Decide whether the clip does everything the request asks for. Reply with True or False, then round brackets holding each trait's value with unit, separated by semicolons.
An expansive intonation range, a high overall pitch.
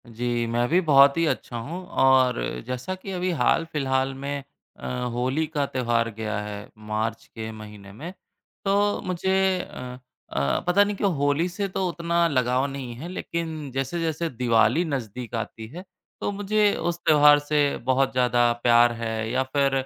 False (6.0 semitones; 135 Hz)